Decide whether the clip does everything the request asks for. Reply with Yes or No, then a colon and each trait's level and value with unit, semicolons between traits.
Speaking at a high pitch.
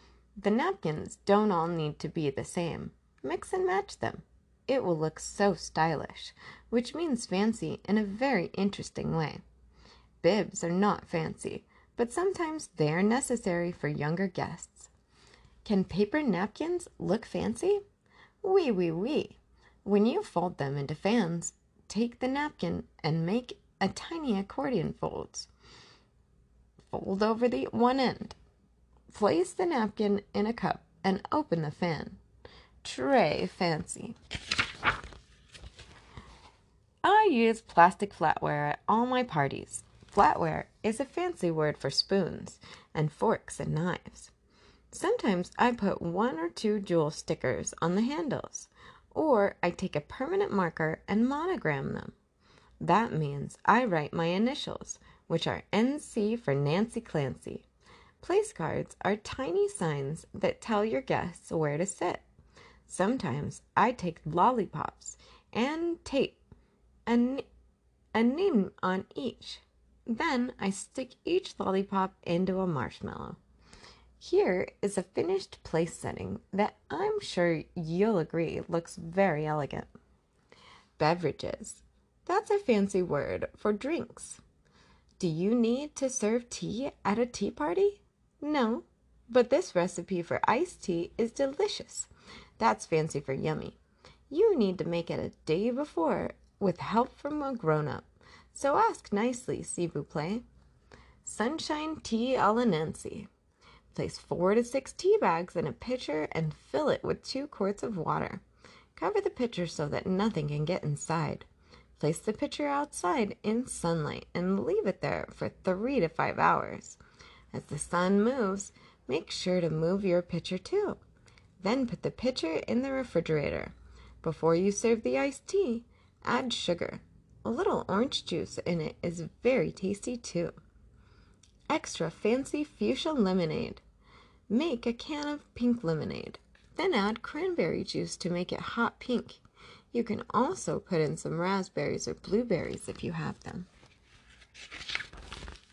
Yes: high, 205 Hz